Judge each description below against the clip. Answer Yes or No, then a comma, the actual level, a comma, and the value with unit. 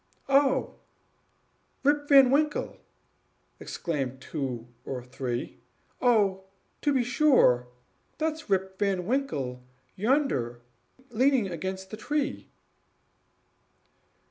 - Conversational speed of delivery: No, slow, 90 wpm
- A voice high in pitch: Yes, high, 205 Hz